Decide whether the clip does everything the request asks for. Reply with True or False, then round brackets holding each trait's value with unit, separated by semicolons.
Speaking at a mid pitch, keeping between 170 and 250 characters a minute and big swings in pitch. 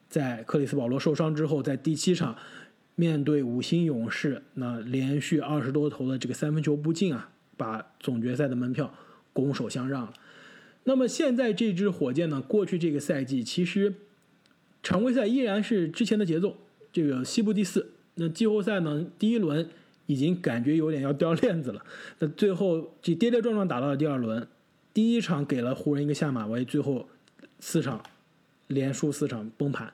False (155 Hz; 275 characters per minute; 6.1 semitones)